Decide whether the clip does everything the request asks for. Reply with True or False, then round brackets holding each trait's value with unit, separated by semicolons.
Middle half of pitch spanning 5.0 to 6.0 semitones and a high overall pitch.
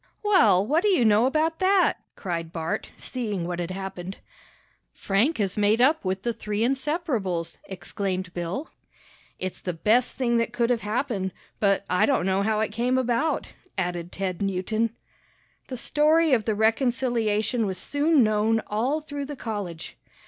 True (5.3 semitones; 220 Hz)